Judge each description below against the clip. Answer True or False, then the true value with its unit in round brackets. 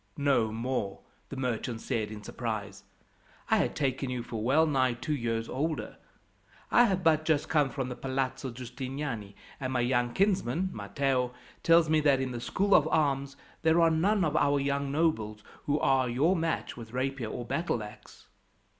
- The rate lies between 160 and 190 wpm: True (170 wpm)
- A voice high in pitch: False (135 Hz)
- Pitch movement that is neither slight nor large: True (4.4 semitones)